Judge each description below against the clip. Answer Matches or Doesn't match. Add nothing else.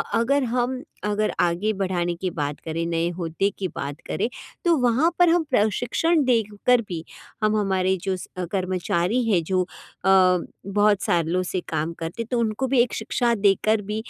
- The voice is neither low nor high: Doesn't match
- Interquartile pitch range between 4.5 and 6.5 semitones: Matches